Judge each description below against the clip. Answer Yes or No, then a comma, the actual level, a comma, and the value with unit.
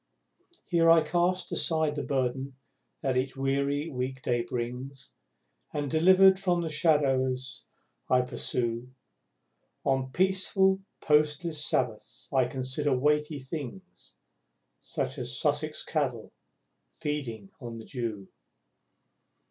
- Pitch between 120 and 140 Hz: Yes, low, 135 Hz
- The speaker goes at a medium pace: No, slow, 110 wpm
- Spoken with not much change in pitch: No, average, 3.8 semitones